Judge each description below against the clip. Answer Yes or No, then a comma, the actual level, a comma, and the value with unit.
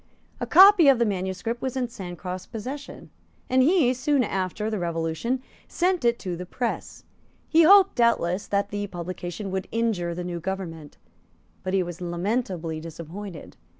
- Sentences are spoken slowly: No, average, 155 wpm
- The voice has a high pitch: Yes, high, 200 Hz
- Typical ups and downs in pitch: No, wide, 5.9 semitones